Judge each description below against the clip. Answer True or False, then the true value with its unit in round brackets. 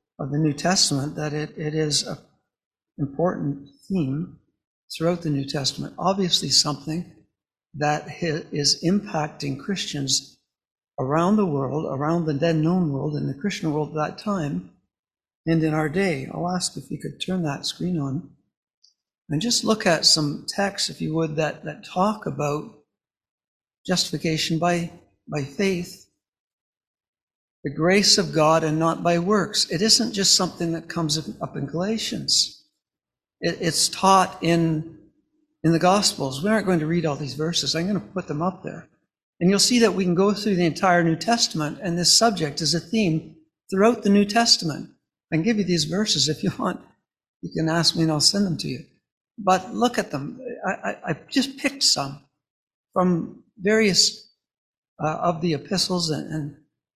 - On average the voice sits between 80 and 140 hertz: False (165 Hz)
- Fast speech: False (170 wpm)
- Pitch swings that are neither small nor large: True (4.2 semitones)